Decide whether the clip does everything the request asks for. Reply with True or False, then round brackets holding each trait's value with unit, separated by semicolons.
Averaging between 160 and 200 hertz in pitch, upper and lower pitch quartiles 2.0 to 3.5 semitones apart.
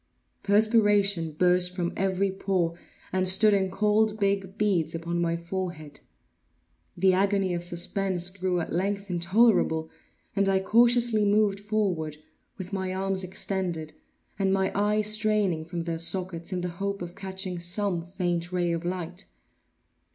True (190 Hz; 2.5 semitones)